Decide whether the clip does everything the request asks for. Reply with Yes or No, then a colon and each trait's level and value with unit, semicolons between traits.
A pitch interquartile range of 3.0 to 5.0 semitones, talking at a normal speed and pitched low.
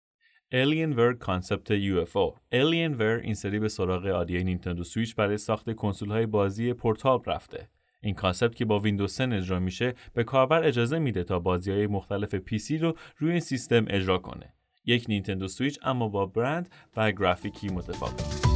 No: average, 4.4 semitones; fast, 170 wpm; low, 110 Hz